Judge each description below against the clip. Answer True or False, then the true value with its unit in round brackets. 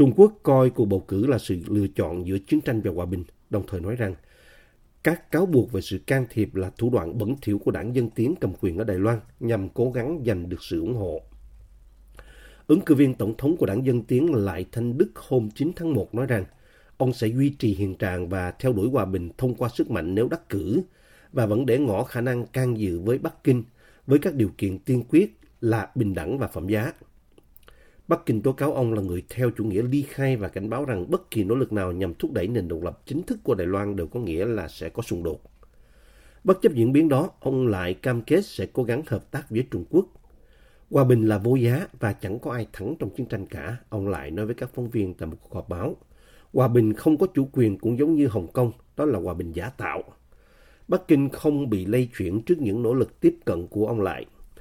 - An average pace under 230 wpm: False (245 wpm)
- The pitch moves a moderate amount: True (4.9 semitones)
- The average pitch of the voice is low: True (115 Hz)